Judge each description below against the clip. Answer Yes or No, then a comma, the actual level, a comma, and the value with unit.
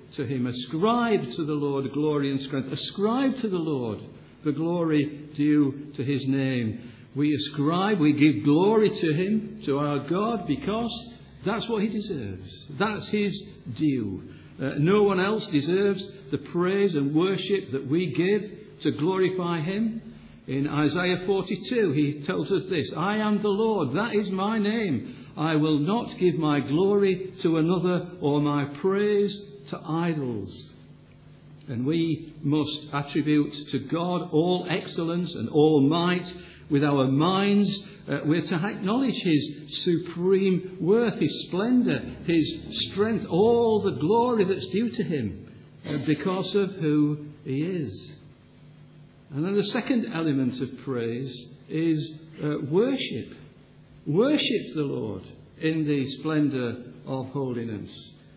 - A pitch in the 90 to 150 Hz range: No, medium, 160 Hz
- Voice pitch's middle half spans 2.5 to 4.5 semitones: No, wide, 5.5 semitones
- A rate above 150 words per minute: No, average, 140 wpm